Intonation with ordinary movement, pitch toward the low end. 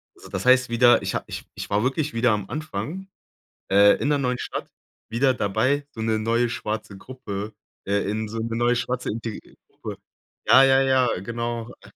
Yes: average, 3.0 semitones; low, 120 Hz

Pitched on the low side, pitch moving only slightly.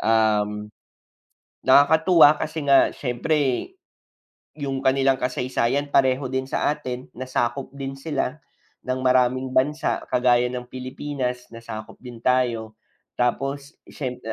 Yes: low, 130 Hz; narrow, 1.9 semitones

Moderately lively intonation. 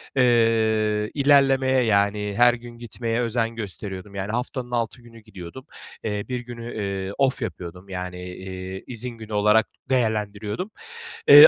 Yes: average, 3.2 semitones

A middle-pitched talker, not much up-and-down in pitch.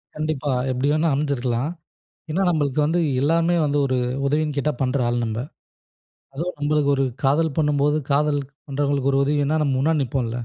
Yes: medium, 145 Hz; narrow, 2.1 semitones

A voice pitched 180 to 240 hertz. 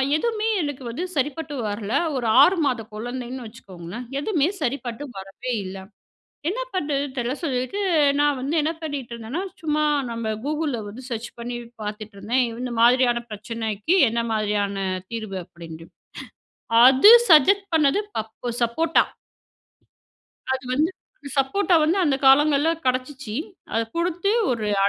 No: very high, 255 Hz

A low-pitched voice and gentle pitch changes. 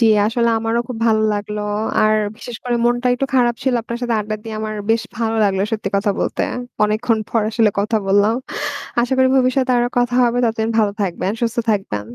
No: high, 225 Hz; narrow, 2.2 semitones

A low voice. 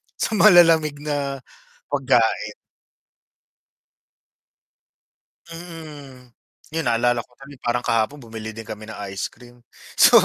Yes: low, 130 Hz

